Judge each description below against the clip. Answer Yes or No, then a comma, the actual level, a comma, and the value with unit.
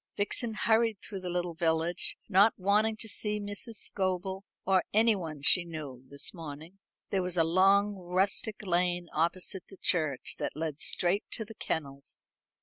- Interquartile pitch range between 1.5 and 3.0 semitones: No, average, 3.7 semitones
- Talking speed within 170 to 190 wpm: No, average, 155 wpm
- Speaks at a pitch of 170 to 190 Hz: Yes, medium, 185 Hz